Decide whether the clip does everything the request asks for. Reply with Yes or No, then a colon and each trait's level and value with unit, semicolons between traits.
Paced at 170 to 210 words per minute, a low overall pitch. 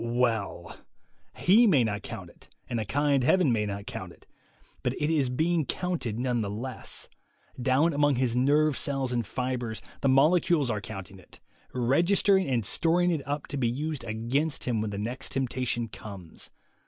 Yes: average, 175 wpm; low, 130 Hz